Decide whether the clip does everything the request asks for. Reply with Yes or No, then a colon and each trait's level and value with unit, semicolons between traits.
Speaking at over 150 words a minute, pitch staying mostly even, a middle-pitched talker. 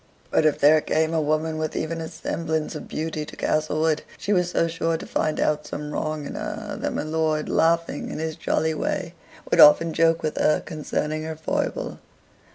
Yes: average, 195 wpm; narrow, 0.9 semitones; medium, 155 Hz